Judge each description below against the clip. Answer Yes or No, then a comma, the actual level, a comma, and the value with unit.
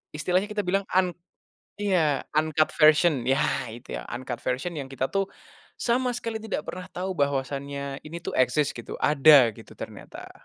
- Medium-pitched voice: Yes, medium, 155 Hz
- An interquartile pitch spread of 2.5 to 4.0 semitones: No, wide, 5.4 semitones